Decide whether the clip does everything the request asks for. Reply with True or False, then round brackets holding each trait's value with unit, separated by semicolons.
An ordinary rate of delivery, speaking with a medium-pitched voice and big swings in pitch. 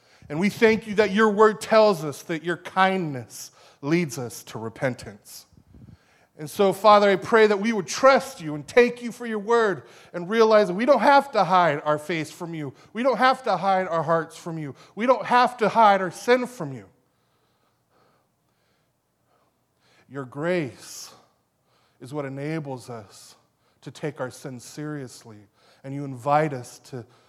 True (170 wpm; 165 Hz; 7.5 semitones)